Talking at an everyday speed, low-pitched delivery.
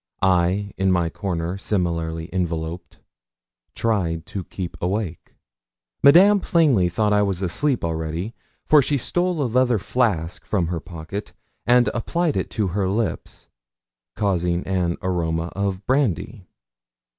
No: slow, 130 wpm; very low, 95 Hz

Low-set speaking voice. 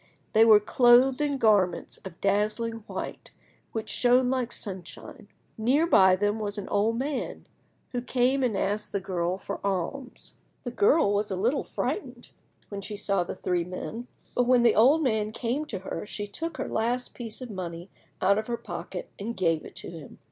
No: high, 220 Hz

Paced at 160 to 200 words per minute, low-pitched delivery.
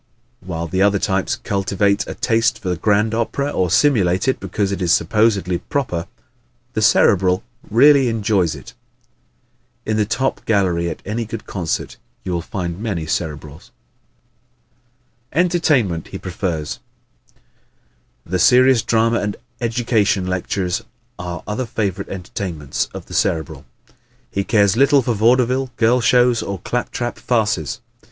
No: slow, 135 wpm; low, 100 Hz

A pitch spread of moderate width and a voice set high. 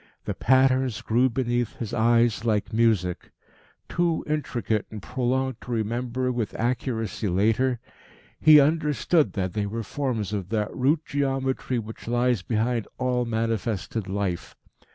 No: average, 3.1 semitones; low, 120 Hz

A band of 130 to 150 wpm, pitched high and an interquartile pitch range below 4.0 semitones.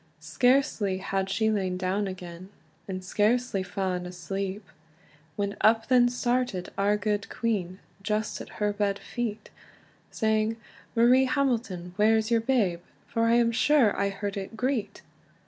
Yes: average, 140 wpm; high, 210 Hz; average, 3.3 semitones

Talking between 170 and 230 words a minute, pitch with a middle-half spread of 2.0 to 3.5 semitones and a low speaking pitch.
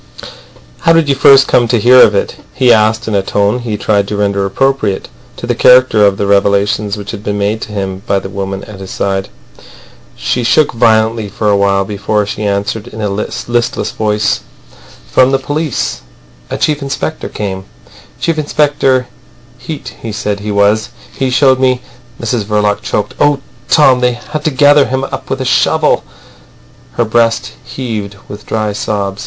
No: average, 180 wpm; average, 4.0 semitones; low, 110 Hz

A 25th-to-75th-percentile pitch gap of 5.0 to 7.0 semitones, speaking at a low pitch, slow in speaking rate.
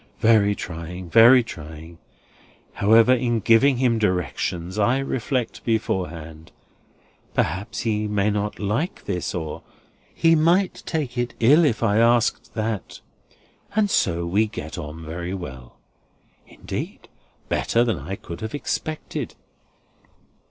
Yes: wide, 5.6 semitones; low, 105 Hz; slow, 125 wpm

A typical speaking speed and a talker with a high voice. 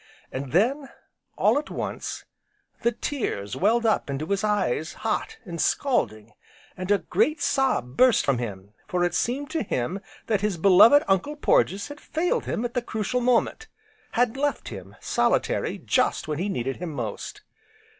Yes: average, 165 wpm; high, 200 Hz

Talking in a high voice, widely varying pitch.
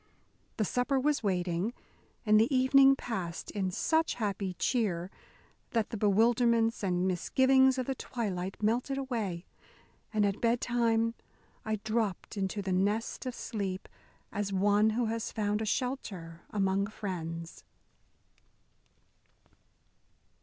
No: high, 215 Hz; average, 3.8 semitones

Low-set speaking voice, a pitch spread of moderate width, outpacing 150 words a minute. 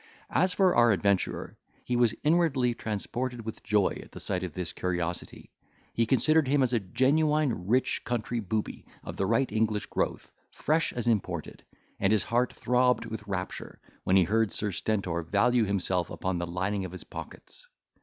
Yes: low, 110 Hz; average, 4.7 semitones; average, 170 wpm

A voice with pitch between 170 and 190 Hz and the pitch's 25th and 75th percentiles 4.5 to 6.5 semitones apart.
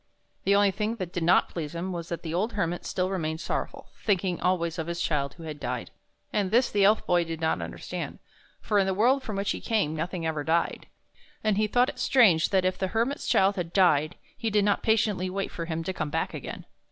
No: medium, 185 Hz; average, 3.7 semitones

